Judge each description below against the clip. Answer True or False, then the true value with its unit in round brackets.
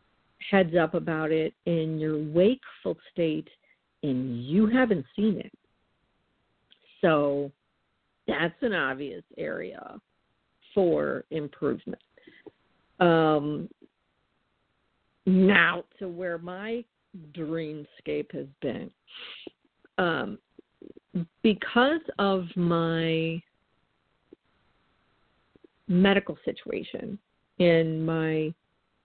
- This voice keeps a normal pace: False (75 wpm)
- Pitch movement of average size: True (3.8 semitones)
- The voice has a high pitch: False (165 Hz)